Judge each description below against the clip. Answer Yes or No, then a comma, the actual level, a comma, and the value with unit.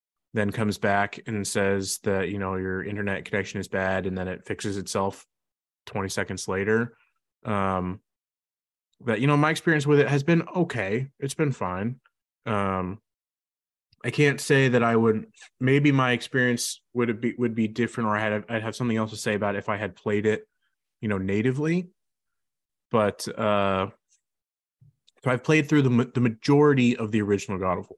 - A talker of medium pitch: No, low, 110 Hz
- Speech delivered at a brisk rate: No, average, 180 wpm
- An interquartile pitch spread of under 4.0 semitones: No, average, 4.3 semitones